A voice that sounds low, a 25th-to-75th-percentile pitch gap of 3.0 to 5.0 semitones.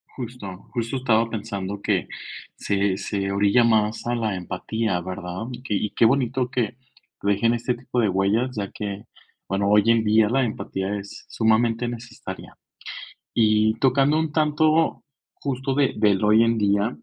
Yes: low, 110 Hz; average, 3.4 semitones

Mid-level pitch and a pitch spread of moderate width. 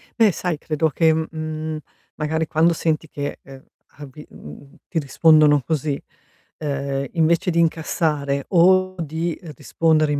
No: medium, 155 Hz; narrow, 2.1 semitones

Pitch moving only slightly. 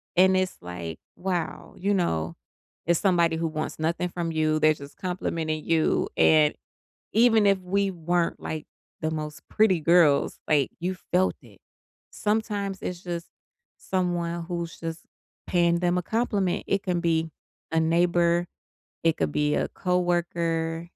Yes: narrow, 2.2 semitones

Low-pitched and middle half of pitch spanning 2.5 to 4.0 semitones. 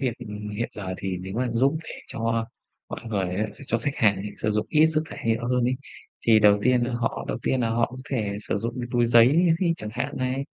Yes: low, 115 Hz; average, 3.3 semitones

